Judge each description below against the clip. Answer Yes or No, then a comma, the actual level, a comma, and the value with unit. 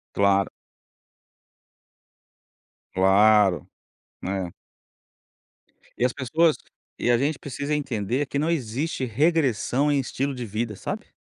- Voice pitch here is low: Yes, low, 125 Hz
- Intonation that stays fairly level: No, wide, 5.4 semitones